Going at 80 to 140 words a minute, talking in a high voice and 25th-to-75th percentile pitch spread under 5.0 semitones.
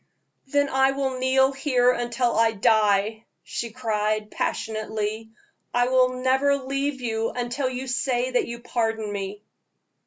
Yes: slow, 135 wpm; high, 245 Hz; average, 3.0 semitones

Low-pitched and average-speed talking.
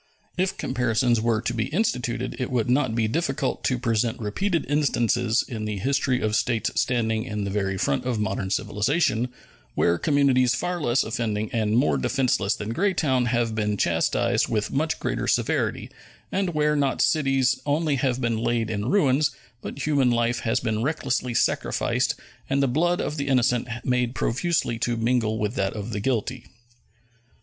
Yes: low, 120 Hz; average, 170 wpm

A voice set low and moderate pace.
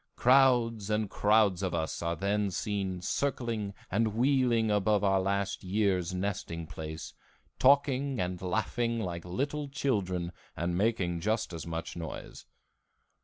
No: low, 100 Hz; slow, 130 wpm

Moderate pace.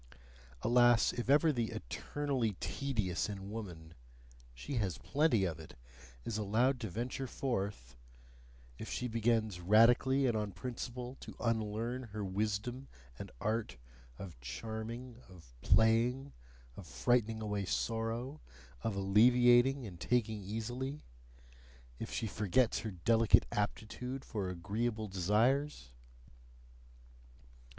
No: slow, 115 wpm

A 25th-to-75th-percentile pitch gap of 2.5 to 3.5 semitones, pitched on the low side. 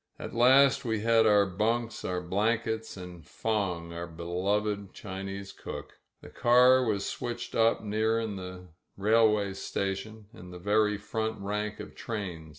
Yes: average, 2.8 semitones; low, 105 Hz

